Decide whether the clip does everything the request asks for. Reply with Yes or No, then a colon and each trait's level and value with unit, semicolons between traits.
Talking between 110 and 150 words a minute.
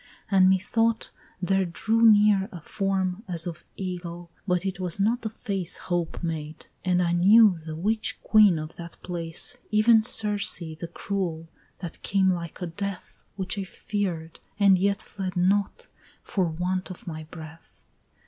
No: average, 160 wpm